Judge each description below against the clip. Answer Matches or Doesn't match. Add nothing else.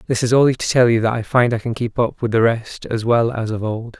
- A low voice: Matches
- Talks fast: Matches